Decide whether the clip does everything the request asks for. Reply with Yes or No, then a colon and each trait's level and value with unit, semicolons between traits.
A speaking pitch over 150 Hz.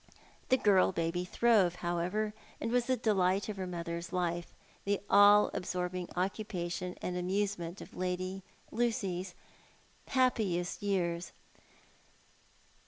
Yes: medium, 185 Hz